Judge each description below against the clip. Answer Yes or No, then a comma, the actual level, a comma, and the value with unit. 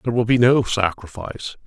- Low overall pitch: Yes, low, 110 Hz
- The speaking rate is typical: Yes, average, 180 wpm